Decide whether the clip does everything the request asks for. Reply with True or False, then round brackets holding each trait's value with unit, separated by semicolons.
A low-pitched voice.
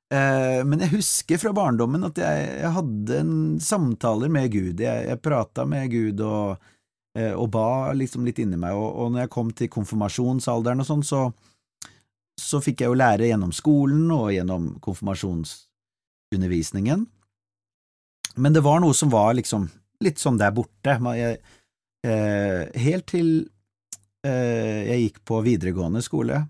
True (115 Hz)